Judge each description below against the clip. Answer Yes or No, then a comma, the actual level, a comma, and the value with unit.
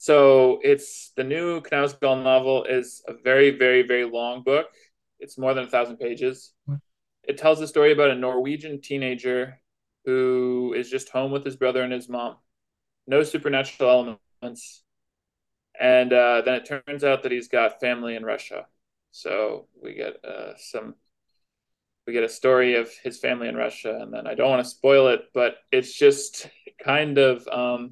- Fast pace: No, average, 170 wpm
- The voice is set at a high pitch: No, low, 130 Hz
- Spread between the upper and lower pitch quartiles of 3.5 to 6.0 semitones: No, narrow, 2.5 semitones